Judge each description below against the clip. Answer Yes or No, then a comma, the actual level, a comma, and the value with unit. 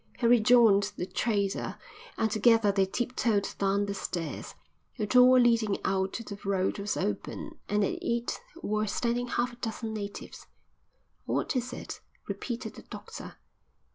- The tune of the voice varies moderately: Yes, average, 3.1 semitones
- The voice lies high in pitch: Yes, high, 215 Hz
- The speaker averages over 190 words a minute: No, average, 150 wpm